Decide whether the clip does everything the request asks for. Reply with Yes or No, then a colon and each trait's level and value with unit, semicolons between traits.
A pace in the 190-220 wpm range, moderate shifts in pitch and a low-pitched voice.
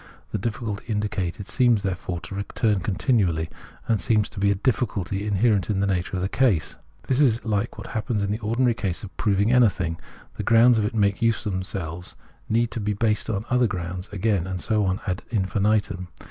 Yes: average, 200 wpm; average, 3.2 semitones; low, 105 Hz